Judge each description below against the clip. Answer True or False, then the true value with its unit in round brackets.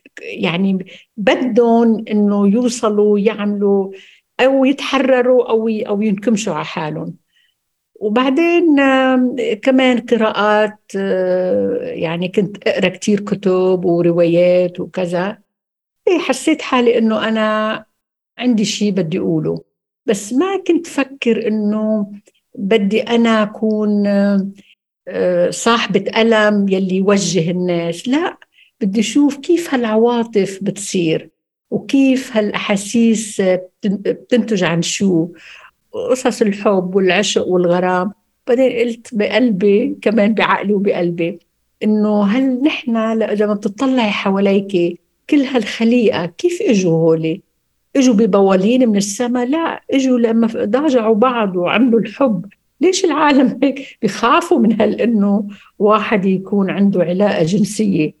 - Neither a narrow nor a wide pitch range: True (4.1 semitones)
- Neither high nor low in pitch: False (215 Hz)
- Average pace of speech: True (100 wpm)